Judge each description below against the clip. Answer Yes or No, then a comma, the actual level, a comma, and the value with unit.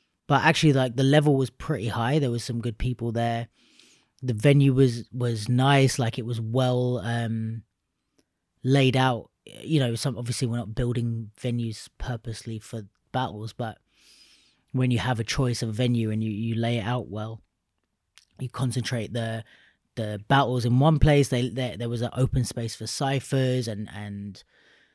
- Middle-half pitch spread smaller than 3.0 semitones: Yes, narrow, 2.4 semitones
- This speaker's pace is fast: No, average, 170 wpm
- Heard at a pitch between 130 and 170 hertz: No, low, 120 Hz